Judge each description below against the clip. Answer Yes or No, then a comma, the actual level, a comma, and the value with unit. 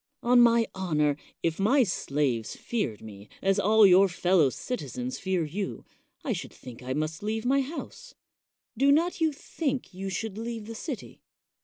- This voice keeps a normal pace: Yes, average, 170 wpm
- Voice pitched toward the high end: Yes, high, 205 Hz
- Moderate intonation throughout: No, wide, 7.5 semitones